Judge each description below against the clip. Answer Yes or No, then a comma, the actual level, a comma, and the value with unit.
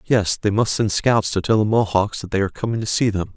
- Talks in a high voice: No, low, 105 Hz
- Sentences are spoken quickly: Yes, fast, 285 wpm